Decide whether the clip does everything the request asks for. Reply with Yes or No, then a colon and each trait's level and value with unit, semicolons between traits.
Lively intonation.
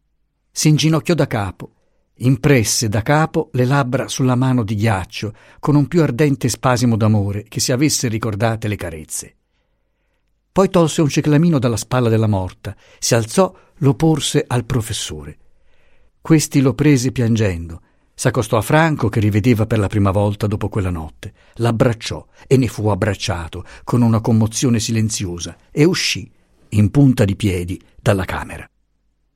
No: average, 4.9 semitones